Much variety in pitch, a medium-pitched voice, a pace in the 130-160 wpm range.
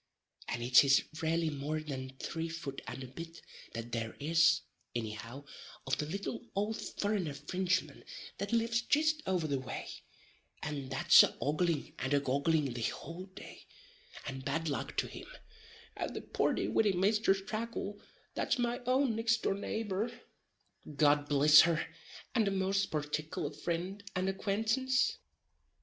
Yes: wide, 6.3 semitones; medium, 165 Hz; average, 150 wpm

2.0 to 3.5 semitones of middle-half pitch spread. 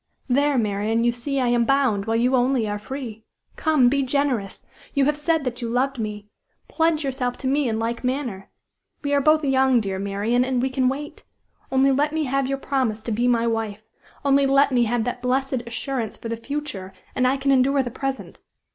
Yes: average, 3.1 semitones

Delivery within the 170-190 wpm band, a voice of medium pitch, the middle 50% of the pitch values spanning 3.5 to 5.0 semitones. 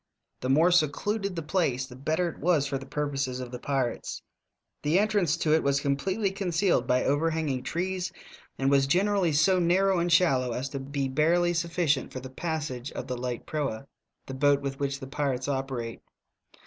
Yes: average, 185 wpm; medium, 145 Hz; average, 4.6 semitones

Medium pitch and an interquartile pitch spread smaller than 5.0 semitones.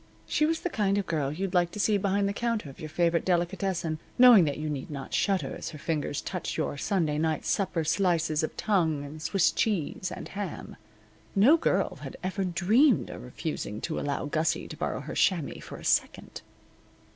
Yes: medium, 175 Hz; average, 4.4 semitones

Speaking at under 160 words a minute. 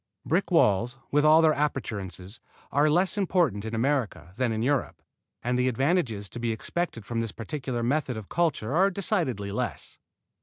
No: average, 165 wpm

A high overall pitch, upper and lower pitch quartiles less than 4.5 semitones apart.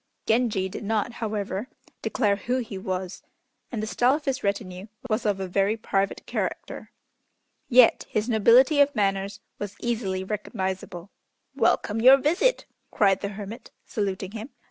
Yes: high, 210 Hz; average, 3.5 semitones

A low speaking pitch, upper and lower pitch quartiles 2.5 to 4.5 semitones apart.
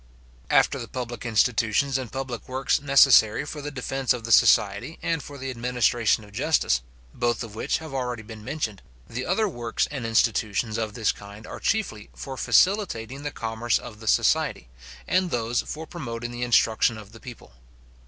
Yes: low, 120 Hz; average, 3.5 semitones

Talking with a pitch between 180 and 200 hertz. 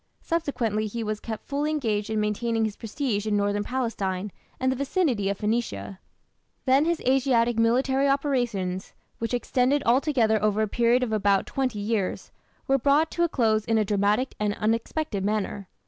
No: high, 230 Hz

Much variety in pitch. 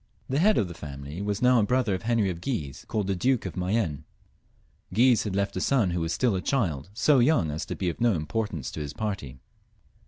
Yes: wide, 6.1 semitones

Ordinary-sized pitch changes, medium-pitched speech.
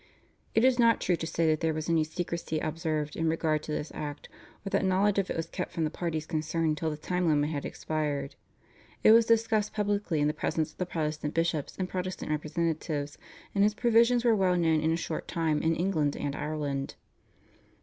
Yes: average, 3.5 semitones; medium, 165 Hz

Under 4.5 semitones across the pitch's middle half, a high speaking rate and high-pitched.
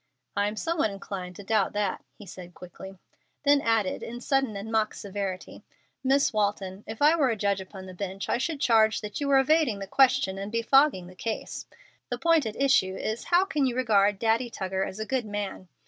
No: average, 5.1 semitones; fast, 210 wpm; high, 215 Hz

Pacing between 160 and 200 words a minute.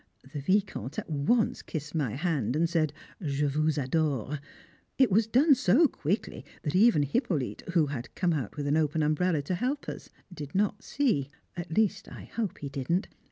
Yes: average, 180 wpm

